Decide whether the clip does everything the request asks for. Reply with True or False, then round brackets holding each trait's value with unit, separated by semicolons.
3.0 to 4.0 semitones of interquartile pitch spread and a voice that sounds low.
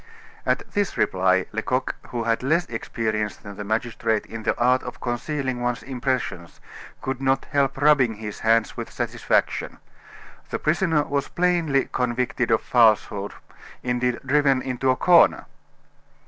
True (3.4 semitones; 125 Hz)